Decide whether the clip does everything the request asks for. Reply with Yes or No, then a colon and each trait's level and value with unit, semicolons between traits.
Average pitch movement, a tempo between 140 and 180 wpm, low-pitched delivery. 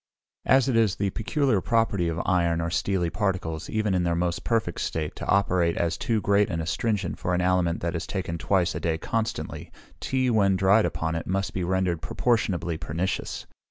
No: average, 3.6 semitones; average, 195 wpm; very low, 90 Hz